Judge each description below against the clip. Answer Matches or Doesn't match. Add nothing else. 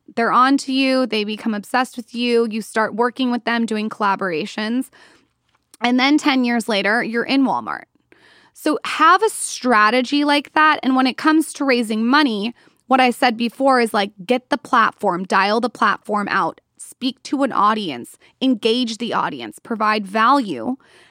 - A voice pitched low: Doesn't match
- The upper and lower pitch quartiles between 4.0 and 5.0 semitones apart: Doesn't match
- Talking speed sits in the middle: Matches